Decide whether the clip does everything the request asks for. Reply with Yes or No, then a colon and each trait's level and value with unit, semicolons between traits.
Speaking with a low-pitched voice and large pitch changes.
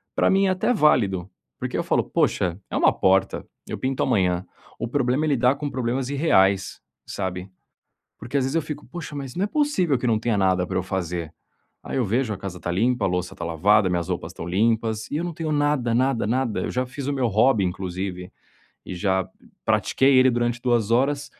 Yes: low, 115 Hz; wide, 6.2 semitones